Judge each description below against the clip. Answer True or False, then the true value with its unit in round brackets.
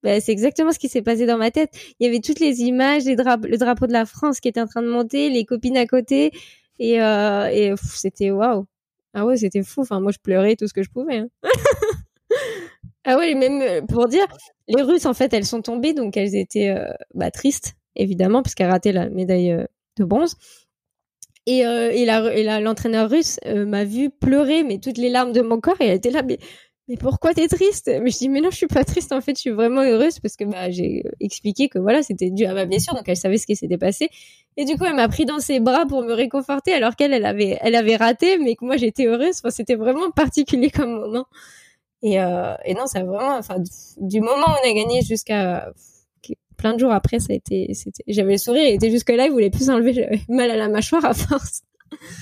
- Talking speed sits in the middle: False (245 wpm)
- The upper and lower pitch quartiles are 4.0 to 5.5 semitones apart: True (4.6 semitones)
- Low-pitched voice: False (240 Hz)